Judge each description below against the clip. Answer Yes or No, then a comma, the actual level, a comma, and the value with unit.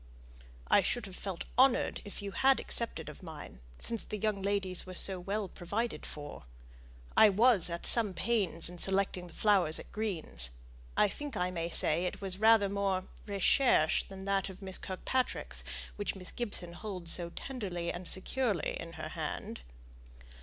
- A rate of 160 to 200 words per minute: Yes, average, 165 wpm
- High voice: Yes, high, 195 Hz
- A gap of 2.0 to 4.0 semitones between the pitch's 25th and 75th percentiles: Yes, average, 3.2 semitones